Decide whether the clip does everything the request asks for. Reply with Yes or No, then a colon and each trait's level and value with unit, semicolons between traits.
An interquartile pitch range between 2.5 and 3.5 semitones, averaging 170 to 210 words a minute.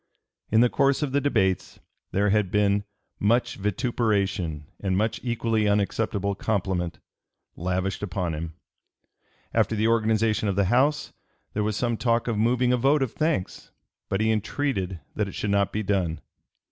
No: average, 3.2 semitones; average, 160 wpm